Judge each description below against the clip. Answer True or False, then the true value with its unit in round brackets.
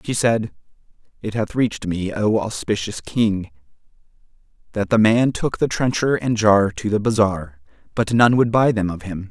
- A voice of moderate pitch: False (110 Hz)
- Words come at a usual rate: True (175 wpm)